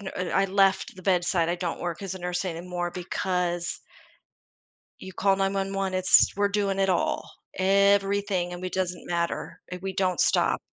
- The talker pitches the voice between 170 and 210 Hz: Yes, medium, 185 Hz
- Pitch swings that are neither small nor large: No, narrow, 1.7 semitones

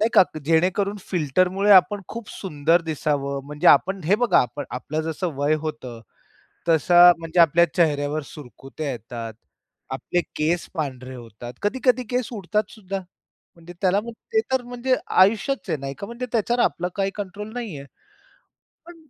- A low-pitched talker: No, medium, 175 Hz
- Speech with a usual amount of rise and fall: No, wide, 6.1 semitones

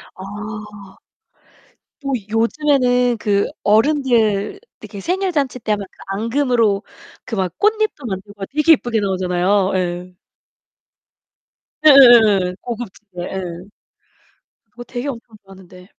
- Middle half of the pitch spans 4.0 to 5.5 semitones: Yes, average, 5.1 semitones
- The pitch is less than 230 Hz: Yes, high, 220 Hz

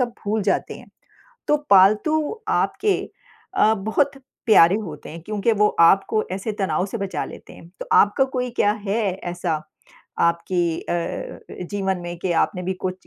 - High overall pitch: Yes, high, 195 Hz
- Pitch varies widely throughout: No, average, 3.8 semitones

